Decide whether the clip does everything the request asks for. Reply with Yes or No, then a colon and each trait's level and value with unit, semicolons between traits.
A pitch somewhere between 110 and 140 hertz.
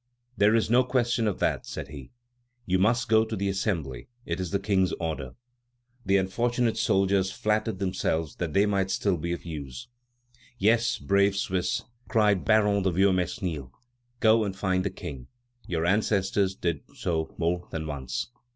No: very low, 95 Hz